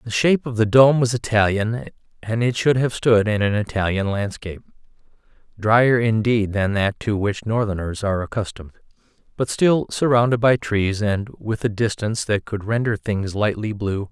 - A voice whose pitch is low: Yes, low, 110 Hz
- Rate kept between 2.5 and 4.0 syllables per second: No, 5.0 syllables/s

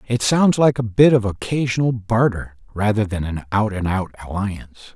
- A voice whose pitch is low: Yes, low, 110 Hz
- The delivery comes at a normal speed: Yes, average, 180 wpm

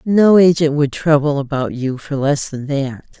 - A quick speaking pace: No, average, 190 wpm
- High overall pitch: No, medium, 145 Hz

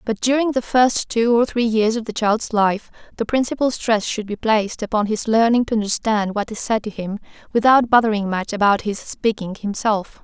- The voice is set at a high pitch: Yes, high, 220 Hz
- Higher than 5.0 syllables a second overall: Yes, 5.2 syllables/s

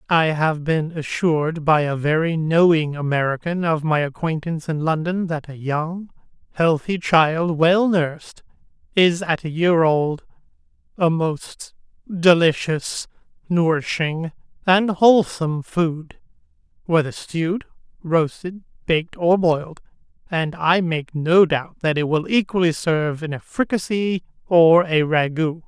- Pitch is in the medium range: Yes, medium, 165 Hz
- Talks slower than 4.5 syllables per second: Yes, 4.1 syllables/s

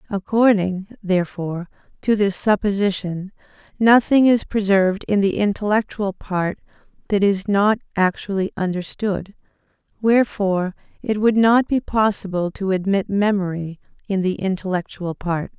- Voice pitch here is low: No, high, 200 Hz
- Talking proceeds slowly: Yes, slow, 115 wpm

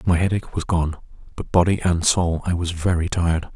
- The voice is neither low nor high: No, very low, 85 Hz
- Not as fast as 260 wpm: Yes, fast, 205 wpm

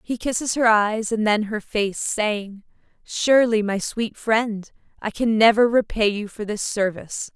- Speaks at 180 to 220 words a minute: No, average, 170 wpm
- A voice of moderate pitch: No, high, 215 Hz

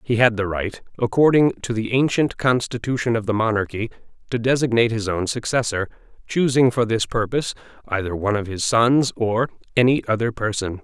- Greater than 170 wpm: No, average, 165 wpm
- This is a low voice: Yes, low, 115 Hz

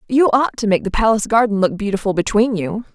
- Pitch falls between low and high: No, high, 215 Hz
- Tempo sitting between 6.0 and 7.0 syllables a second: Yes, 6.3 syllables/s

